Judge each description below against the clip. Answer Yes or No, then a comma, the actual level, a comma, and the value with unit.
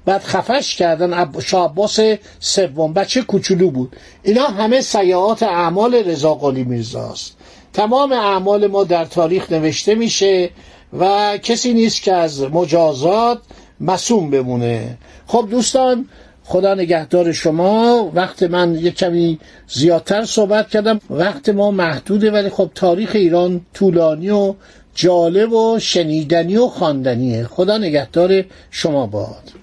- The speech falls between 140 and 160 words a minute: No, average, 120 wpm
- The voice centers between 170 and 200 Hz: Yes, medium, 185 Hz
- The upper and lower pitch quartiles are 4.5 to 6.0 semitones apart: No, average, 4.0 semitones